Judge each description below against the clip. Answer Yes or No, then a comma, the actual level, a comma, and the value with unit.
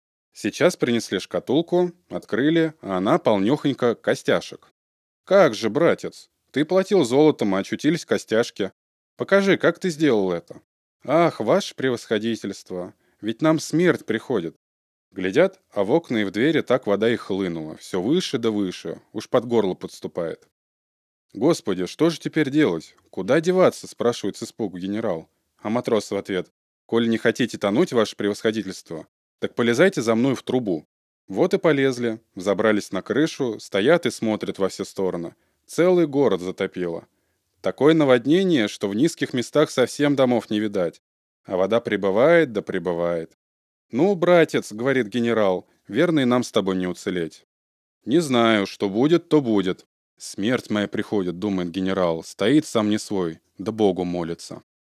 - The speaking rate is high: No, average, 145 wpm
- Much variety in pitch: Yes, wide, 7.2 semitones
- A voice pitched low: Yes, low, 110 Hz